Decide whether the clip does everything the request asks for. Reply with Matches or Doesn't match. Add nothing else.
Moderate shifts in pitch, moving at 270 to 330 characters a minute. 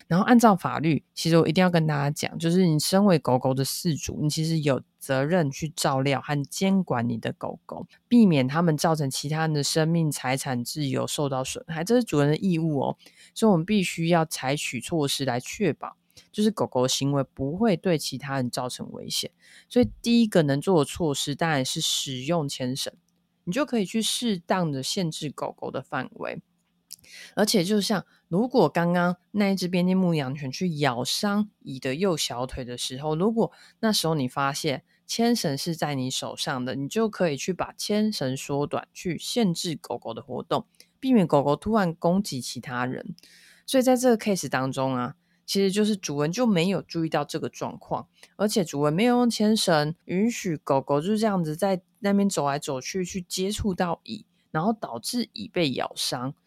Doesn't match